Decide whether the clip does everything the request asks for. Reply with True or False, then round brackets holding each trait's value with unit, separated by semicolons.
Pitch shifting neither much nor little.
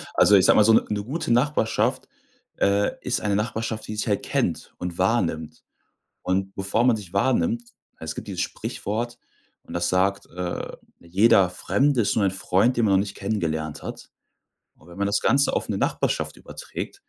True (3.8 semitones)